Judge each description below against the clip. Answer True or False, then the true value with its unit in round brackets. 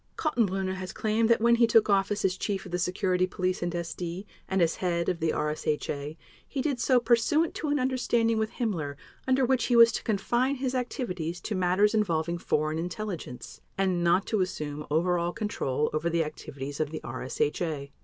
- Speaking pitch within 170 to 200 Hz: True (185 Hz)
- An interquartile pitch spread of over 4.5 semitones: True (5.6 semitones)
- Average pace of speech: True (190 wpm)